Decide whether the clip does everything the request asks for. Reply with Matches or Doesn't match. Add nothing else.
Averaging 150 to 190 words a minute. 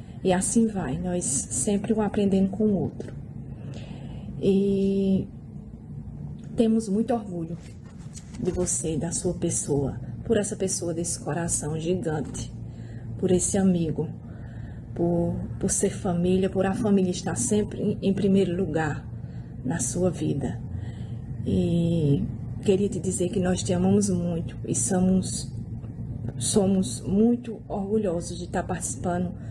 Doesn't match